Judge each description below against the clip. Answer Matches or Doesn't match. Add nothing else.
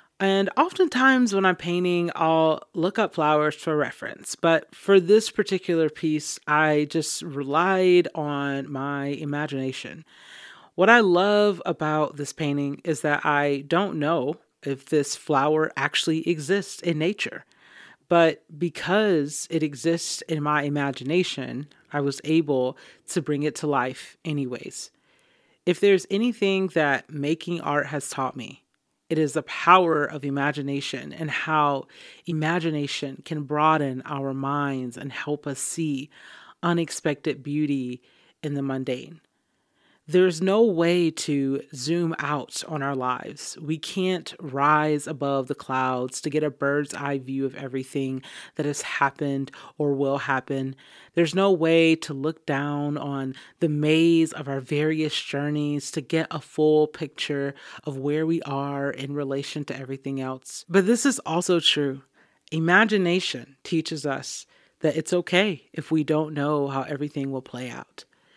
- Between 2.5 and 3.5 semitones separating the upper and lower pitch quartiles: Matches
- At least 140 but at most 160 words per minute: Matches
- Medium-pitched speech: Matches